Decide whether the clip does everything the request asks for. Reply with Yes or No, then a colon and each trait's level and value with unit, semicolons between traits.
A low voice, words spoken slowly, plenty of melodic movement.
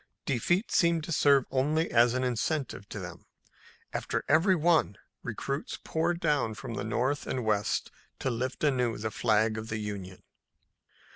No: low, 125 Hz; average, 155 wpm; wide, 5.8 semitones